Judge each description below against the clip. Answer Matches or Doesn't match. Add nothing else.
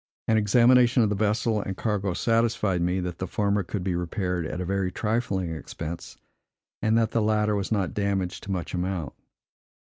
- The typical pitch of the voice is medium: Doesn't match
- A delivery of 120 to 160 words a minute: Doesn't match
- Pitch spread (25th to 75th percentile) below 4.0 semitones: Matches